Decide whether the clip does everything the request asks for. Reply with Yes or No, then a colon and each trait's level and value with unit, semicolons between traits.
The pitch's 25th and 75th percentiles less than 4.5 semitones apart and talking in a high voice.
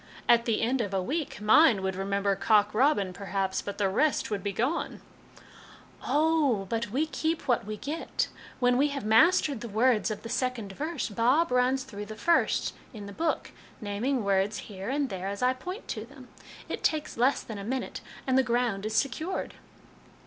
No: average, 5.3 semitones; high, 235 Hz